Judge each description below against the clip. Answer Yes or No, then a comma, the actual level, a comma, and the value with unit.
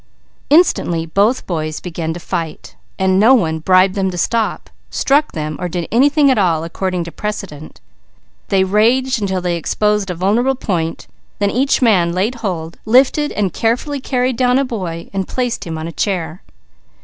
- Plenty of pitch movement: Yes, wide, 6.2 semitones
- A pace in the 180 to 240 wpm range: No, average, 165 wpm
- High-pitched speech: Yes, high, 195 Hz